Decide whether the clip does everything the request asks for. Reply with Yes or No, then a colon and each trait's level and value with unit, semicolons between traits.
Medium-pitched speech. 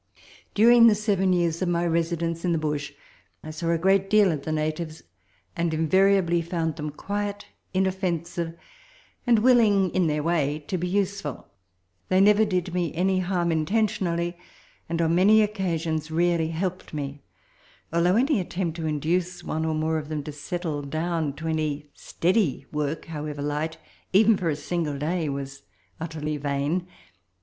Yes: medium, 170 Hz